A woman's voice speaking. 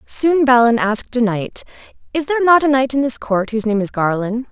Yes: female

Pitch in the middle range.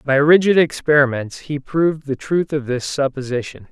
Yes: medium, 145 Hz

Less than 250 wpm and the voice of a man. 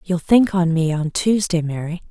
No: average, 200 wpm; female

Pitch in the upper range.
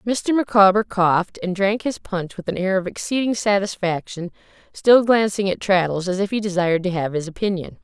Yes: high, 195 Hz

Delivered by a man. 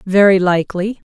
No: female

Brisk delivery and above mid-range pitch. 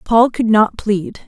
No: average, 190 wpm; high, 215 Hz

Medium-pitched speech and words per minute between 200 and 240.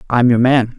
No: low, 120 Hz; fast, 230 wpm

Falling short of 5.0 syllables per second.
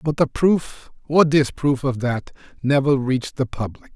Yes: 4.5 syllables/s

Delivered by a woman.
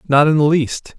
No: male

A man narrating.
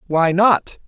Yes: male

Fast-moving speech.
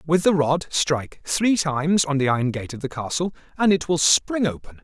Yes: fast, 225 wpm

